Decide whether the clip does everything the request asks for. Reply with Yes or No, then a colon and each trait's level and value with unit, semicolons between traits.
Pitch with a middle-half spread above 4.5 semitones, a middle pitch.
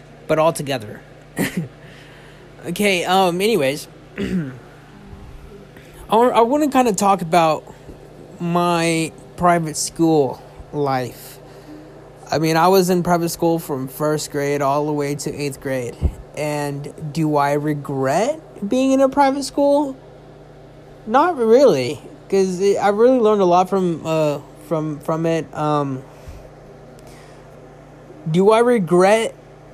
Yes: average, 5.1 semitones; medium, 160 Hz